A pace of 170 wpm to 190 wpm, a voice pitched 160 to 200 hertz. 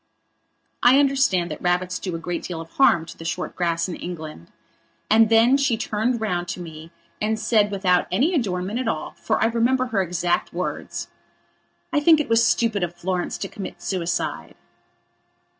Yes: average, 175 wpm; high, 190 Hz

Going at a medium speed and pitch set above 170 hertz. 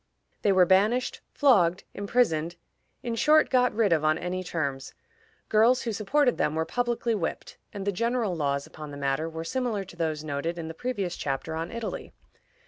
Yes: average, 180 wpm; medium, 185 Hz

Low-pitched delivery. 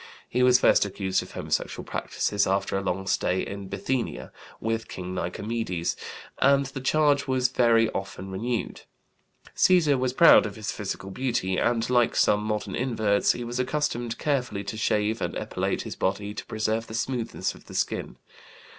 Yes: low, 110 Hz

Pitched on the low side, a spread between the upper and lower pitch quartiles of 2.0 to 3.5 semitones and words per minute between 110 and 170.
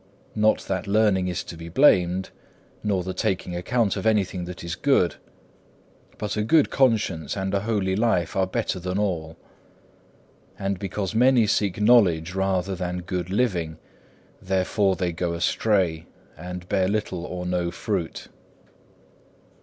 Yes: very low, 95 Hz; average, 2.8 semitones; average, 145 wpm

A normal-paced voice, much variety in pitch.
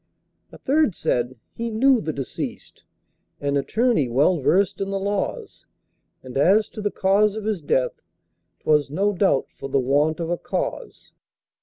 Yes: average, 160 wpm; wide, 6.9 semitones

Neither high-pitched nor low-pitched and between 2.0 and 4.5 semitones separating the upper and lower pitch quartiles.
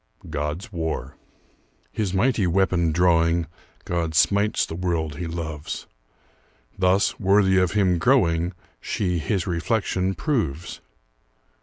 No: very low, 90 Hz; average, 2.8 semitones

